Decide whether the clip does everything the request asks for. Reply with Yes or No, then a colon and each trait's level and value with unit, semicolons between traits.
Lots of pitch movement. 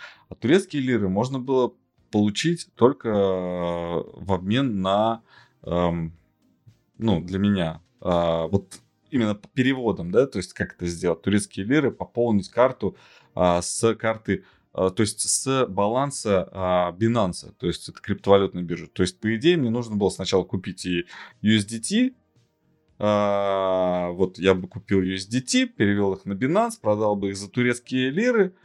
No: average, 4.2 semitones